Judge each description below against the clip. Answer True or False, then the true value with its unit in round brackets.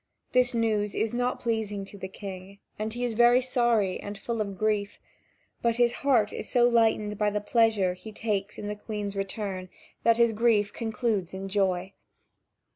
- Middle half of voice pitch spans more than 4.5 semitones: False (2.7 semitones)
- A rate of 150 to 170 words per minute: False (180 wpm)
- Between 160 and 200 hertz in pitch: False (215 Hz)